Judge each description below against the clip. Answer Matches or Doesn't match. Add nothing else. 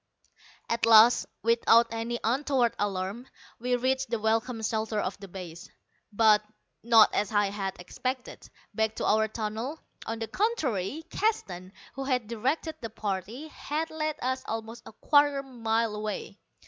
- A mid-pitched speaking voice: Doesn't match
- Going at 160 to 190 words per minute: Doesn't match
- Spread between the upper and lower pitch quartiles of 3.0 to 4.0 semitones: Matches